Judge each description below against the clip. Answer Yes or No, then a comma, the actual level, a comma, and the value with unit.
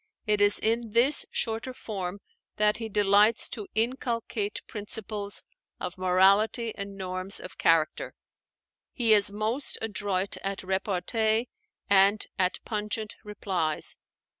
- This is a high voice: Yes, high, 210 Hz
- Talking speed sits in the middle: No, slow, 115 wpm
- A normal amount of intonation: No, narrow, 2.3 semitones